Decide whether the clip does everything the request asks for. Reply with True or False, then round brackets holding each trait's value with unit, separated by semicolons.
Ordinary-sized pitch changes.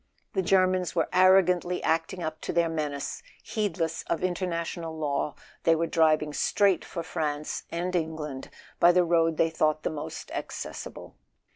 False (2.3 semitones)